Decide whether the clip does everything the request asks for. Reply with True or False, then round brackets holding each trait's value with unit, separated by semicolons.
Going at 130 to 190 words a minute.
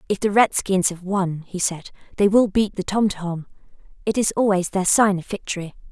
False (205 wpm)